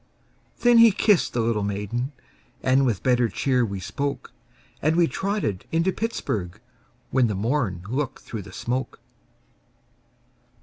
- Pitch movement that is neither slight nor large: No, wide, 6.7 semitones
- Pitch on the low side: Yes, low, 125 Hz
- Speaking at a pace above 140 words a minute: No, slow, 135 wpm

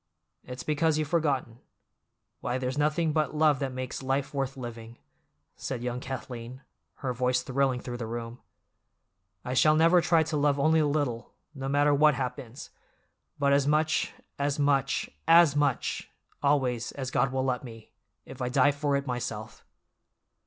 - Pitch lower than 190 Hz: Yes, low, 135 Hz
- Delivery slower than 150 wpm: No, average, 160 wpm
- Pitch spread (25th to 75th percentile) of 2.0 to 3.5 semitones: Yes, average, 2.8 semitones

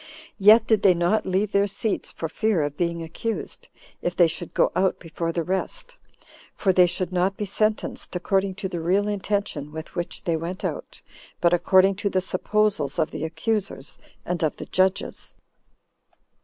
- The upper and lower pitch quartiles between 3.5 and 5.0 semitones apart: No, average, 3.1 semitones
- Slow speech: No, average, 175 wpm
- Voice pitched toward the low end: No, medium, 185 Hz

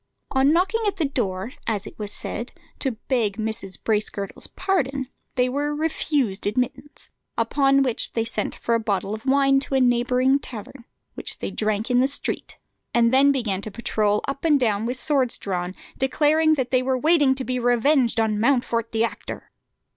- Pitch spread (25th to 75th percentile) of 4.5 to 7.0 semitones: No, average, 3.9 semitones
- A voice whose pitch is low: No, very high, 250 Hz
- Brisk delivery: No, average, 175 wpm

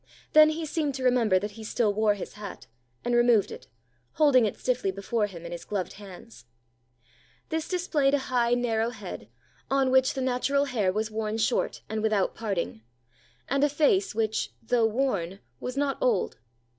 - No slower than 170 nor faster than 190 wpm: Yes, average, 175 wpm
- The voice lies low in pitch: No, high, 235 Hz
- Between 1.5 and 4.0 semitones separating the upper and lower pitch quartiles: No, average, 4.8 semitones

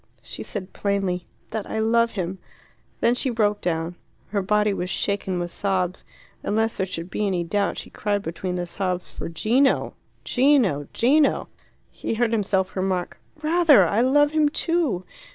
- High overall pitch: Yes, high, 200 Hz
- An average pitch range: Yes, average, 4.3 semitones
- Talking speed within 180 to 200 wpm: No, average, 165 wpm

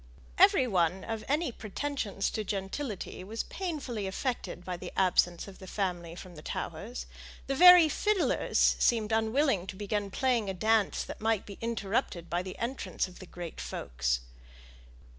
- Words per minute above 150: Yes, average, 160 wpm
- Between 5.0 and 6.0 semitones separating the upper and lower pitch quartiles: No, average, 4.5 semitones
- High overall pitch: Yes, high, 205 Hz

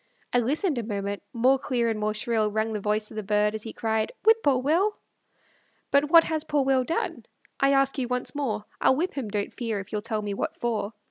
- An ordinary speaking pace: No, fast, 230 wpm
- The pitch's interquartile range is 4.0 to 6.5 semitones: Yes, average, 4.4 semitones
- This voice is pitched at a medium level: No, high, 235 Hz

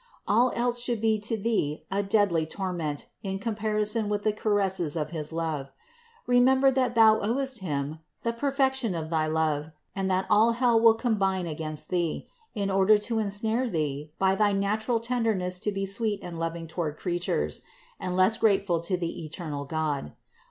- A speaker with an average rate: Yes, average, 170 wpm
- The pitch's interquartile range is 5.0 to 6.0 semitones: Yes, average, 5.3 semitones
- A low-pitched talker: No, high, 195 Hz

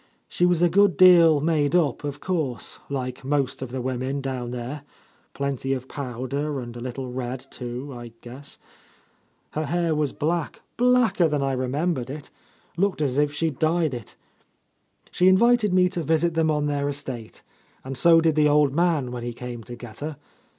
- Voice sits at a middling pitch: Yes, medium, 145 Hz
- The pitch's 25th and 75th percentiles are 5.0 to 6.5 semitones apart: No, average, 4.2 semitones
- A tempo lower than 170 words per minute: No, average, 185 wpm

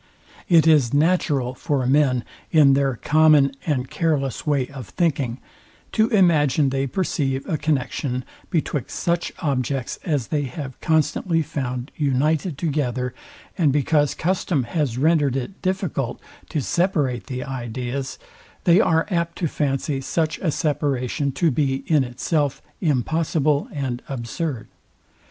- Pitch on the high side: No, medium, 145 Hz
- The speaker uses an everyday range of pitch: Yes, average, 3.5 semitones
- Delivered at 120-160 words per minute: Yes, slow, 135 wpm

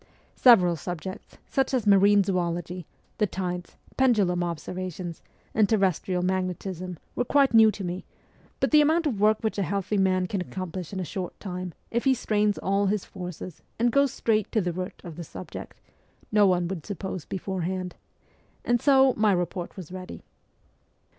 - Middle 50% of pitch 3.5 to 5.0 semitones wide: No, average, 3.1 semitones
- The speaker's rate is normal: Yes, average, 165 wpm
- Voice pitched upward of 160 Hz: Yes, high, 190 Hz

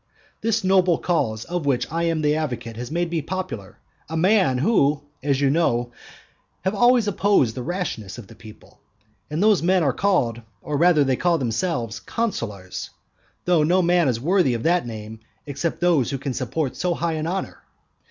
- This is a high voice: No, medium, 155 Hz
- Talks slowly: No, average, 180 wpm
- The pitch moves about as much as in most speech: No, wide, 6.5 semitones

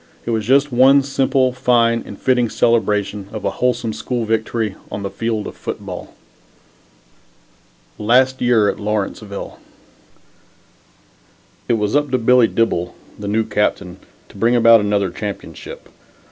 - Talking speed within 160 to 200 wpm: No, slow, 135 wpm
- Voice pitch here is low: Yes, low, 115 Hz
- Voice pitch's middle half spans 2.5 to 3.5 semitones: Yes, average, 3.1 semitones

